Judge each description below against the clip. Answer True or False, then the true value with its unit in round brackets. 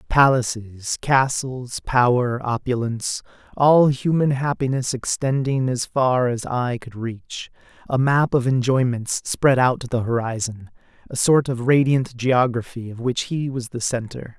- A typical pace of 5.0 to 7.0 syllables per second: False (4.2 syllables/s)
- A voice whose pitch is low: True (125 Hz)